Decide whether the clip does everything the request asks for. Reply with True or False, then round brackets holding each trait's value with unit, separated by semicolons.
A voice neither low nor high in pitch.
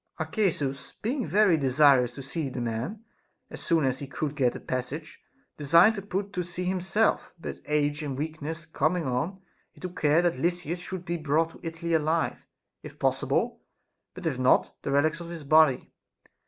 True (155 Hz)